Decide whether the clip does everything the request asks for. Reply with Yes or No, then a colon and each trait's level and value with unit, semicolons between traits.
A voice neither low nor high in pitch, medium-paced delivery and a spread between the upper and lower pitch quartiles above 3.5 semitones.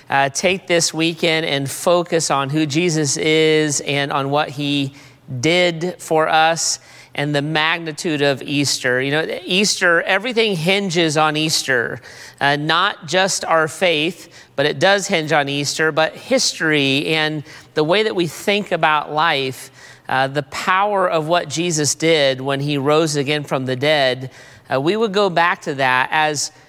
No: medium, 155 Hz; average, 160 wpm; average, 3.2 semitones